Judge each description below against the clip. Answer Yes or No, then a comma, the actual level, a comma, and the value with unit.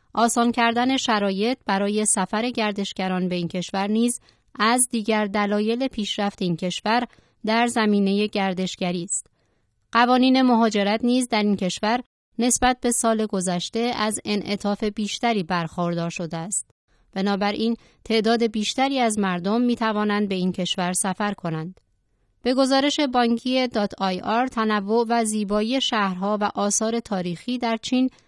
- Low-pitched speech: No, high, 215 Hz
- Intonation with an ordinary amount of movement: Yes, average, 3.2 semitones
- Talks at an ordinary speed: Yes, average, 130 wpm